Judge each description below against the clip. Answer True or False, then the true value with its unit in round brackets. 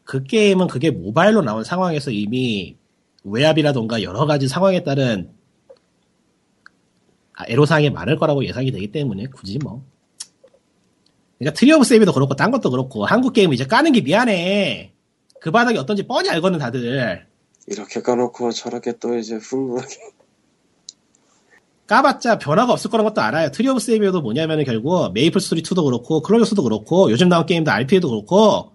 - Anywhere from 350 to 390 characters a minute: True (375 characters per minute)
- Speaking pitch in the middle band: True (160 Hz)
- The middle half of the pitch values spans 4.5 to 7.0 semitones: False (8.3 semitones)